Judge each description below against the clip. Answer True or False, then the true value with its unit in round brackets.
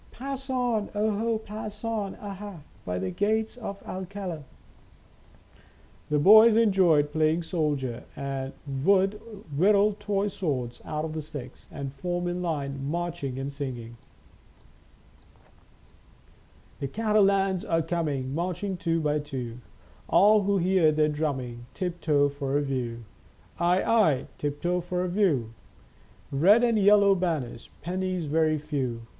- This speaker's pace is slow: True (130 wpm)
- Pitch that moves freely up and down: True (5.9 semitones)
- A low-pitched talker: False (170 Hz)